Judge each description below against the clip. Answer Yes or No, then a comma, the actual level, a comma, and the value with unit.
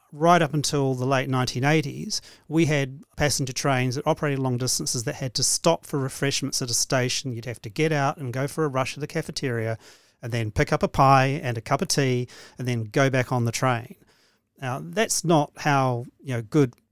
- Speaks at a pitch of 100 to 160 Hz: Yes, low, 135 Hz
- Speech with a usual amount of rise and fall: Yes, average, 3.0 semitones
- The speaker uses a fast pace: Yes, fast, 215 wpm